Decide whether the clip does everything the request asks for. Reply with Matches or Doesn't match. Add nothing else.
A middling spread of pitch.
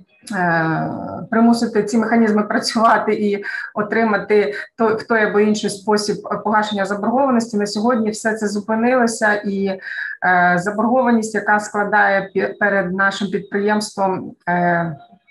Doesn't match